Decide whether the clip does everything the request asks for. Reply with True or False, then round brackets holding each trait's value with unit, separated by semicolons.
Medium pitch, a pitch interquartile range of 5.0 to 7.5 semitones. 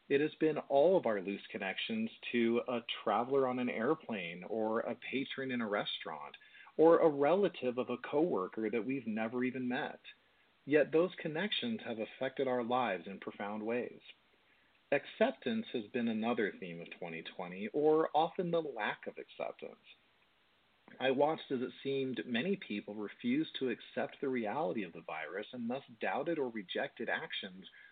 False (130 Hz; 5.6 semitones)